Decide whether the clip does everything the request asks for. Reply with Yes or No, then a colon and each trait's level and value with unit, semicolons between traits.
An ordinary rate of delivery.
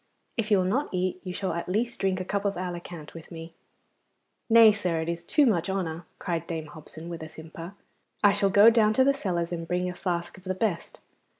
No: fast, 225 wpm